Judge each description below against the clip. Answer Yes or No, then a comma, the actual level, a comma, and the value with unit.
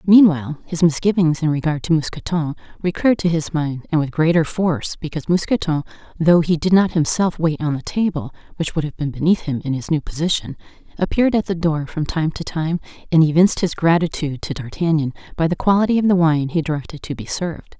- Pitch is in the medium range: Yes, medium, 165 Hz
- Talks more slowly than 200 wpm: No, fast, 205 wpm